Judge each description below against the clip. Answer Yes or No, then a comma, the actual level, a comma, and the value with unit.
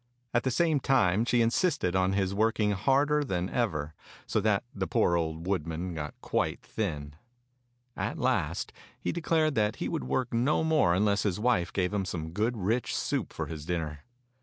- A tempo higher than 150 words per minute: Yes, average, 180 wpm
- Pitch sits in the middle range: No, low, 100 Hz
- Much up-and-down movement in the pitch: Yes, wide, 6.1 semitones